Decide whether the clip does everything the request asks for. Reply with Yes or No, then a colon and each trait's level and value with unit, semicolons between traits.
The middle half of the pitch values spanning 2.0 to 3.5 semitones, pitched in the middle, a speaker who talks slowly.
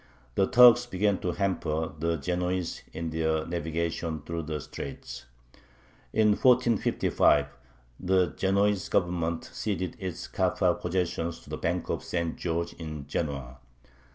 No: average, 3.0 semitones; very low, 85 Hz; slow, 125 wpm